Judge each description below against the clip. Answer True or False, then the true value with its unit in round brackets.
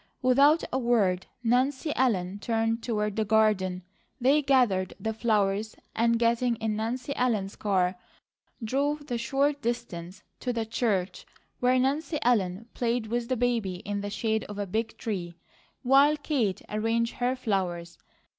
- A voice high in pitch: True (230 Hz)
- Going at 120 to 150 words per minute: True (145 wpm)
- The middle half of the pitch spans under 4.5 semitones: True (3.7 semitones)